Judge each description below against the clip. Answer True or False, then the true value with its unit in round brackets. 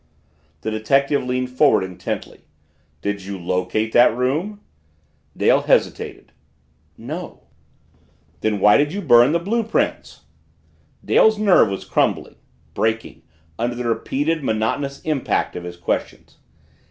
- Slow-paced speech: True (120 wpm)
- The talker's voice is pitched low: True (125 Hz)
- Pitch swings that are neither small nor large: False (5.7 semitones)